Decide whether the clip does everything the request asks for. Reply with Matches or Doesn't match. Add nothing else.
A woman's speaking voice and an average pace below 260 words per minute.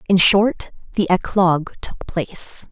Matches